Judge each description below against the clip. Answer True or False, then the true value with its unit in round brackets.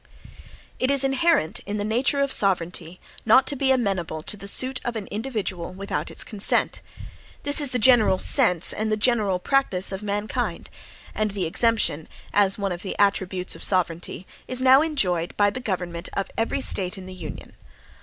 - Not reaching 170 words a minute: False (180 wpm)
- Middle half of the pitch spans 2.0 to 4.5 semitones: False (5.4 semitones)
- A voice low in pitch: False (205 Hz)